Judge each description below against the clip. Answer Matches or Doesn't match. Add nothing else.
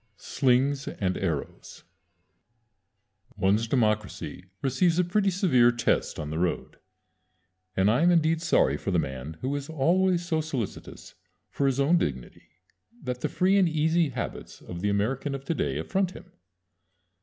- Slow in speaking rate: Doesn't match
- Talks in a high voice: Doesn't match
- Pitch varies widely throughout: Matches